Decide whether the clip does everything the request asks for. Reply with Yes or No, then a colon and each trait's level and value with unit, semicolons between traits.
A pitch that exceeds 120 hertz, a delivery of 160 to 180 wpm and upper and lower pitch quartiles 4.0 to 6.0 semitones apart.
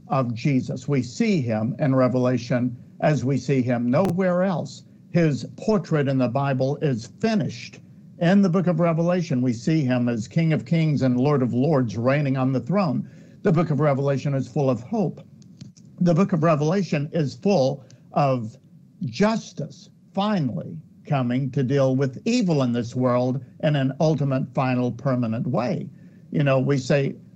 Yes: medium, 140 Hz; average, 165 wpm; average, 5.0 semitones